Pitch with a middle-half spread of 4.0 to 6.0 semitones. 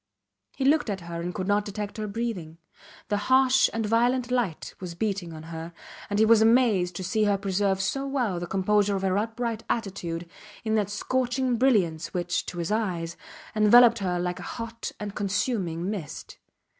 Yes: average, 4.3 semitones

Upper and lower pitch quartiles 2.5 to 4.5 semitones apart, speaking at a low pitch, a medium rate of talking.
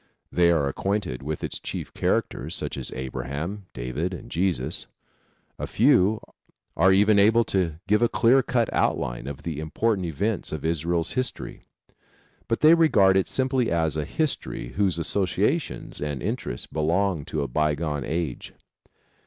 No: wide, 5.6 semitones; very low, 85 Hz; average, 150 wpm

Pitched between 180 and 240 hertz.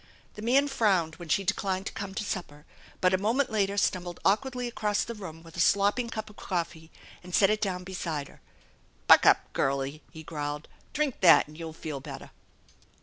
Yes: high, 190 Hz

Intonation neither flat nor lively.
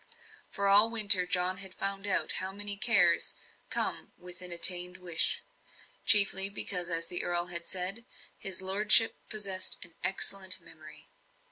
No: narrow, 2.0 semitones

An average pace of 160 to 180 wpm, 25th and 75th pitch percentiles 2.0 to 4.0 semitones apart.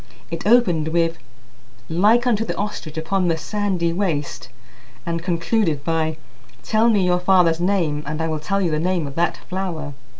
Yes: average, 170 wpm; average, 3.5 semitones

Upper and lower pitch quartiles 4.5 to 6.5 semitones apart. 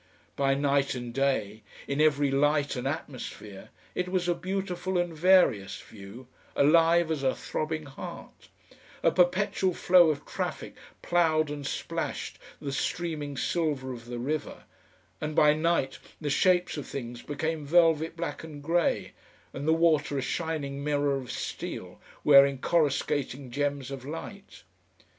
No: average, 3.4 semitones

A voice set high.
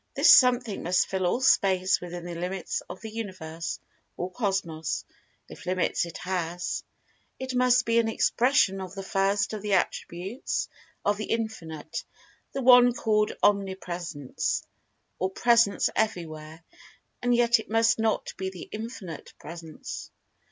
Yes: high, 195 Hz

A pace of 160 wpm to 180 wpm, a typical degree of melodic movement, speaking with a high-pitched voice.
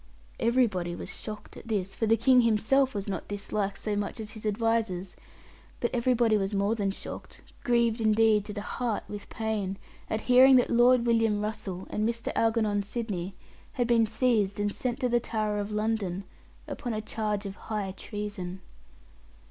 No: average, 170 wpm; narrow, 2.3 semitones; high, 215 Hz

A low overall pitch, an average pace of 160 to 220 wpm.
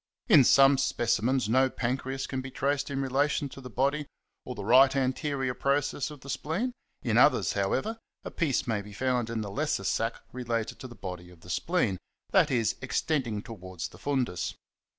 Yes: low, 130 Hz; average, 180 wpm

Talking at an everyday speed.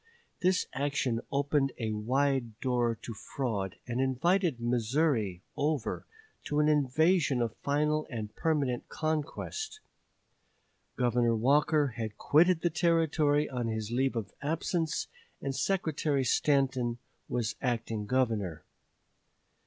No: slow, 115 wpm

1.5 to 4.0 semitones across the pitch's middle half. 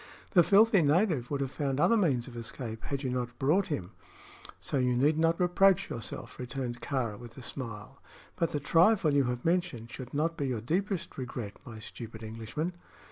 No: wide, 5.6 semitones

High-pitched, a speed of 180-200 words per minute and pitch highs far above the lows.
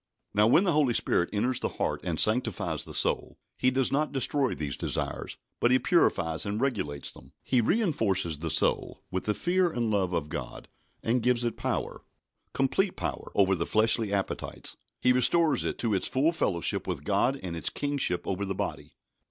No: low, 115 Hz; average, 185 wpm; wide, 6.2 semitones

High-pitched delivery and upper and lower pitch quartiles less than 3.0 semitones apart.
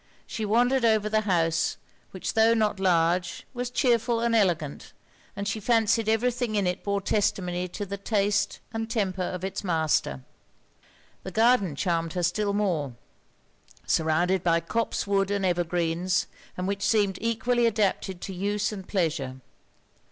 No: high, 200 Hz; average, 3.8 semitones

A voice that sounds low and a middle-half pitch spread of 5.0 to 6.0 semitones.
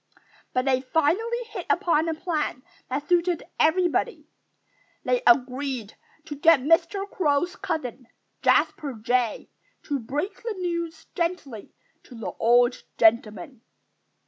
No: very high, 290 Hz; wide, 5.6 semitones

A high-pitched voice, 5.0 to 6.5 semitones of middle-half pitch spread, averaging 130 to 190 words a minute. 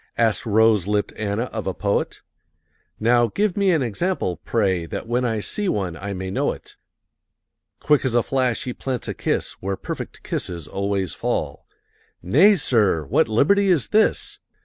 No: low, 110 Hz; average, 5.3 semitones; average, 170 wpm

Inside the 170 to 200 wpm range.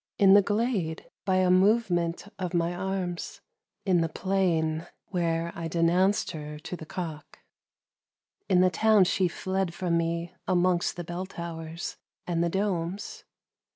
No: average, 140 wpm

